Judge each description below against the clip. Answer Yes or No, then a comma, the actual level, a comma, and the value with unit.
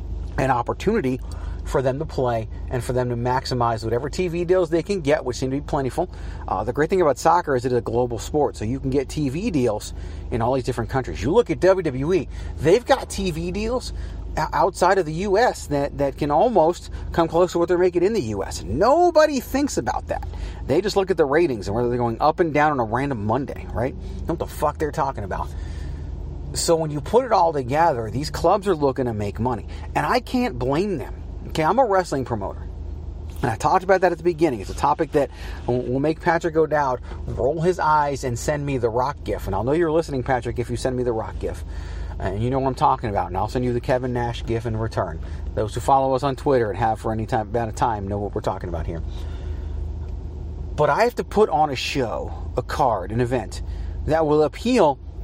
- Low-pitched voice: Yes, low, 125 Hz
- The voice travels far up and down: Yes, wide, 8.1 semitones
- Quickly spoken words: Yes, fast, 230 wpm